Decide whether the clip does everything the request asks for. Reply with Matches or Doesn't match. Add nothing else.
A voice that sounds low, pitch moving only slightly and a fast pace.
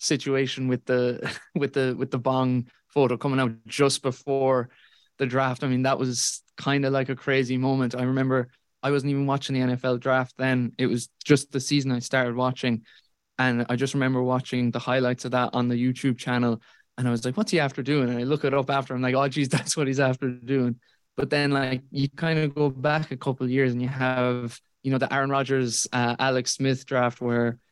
Matches